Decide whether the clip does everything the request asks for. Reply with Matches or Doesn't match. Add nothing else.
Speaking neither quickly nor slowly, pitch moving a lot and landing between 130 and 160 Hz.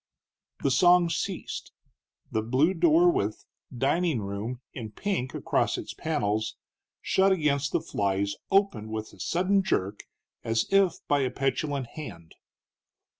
Doesn't match